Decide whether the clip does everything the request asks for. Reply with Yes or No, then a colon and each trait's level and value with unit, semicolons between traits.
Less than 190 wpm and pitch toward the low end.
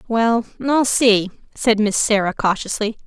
No: slow, 135 wpm; high, 220 Hz